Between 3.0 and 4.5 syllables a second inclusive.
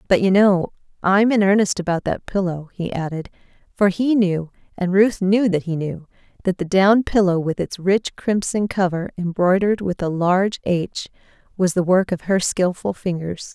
No: 4.8 syllables/s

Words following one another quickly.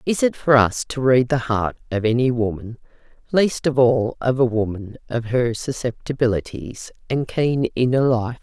No: average, 170 wpm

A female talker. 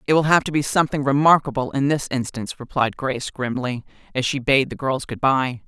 Yes: female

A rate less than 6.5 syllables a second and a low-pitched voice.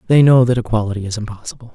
No: 7.6 syllables/s; low, 115 Hz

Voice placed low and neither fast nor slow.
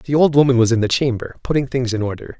No: low, 125 Hz; fast, 275 wpm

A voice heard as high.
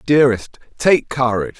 No: low, 130 Hz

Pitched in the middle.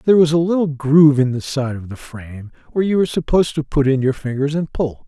Yes: medium, 145 Hz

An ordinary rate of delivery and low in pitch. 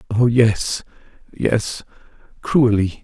No: slow, 80 wpm; low, 115 Hz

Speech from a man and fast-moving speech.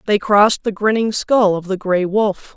No: female; fast, 210 wpm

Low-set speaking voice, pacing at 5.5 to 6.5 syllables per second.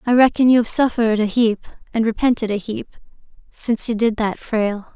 No: high, 225 Hz; 5.7 syllables/s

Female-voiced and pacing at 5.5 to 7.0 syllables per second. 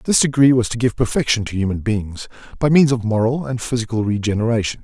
No: male; 6.0 syllables/s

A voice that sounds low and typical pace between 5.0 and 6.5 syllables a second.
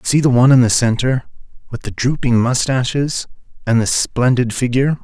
Yes: low, 125 Hz; 5.3 syllables/s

